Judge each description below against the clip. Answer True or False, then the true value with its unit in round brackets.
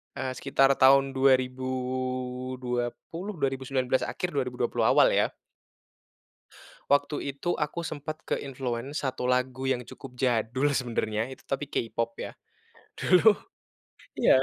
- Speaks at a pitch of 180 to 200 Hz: False (130 Hz)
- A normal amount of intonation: False (1.6 semitones)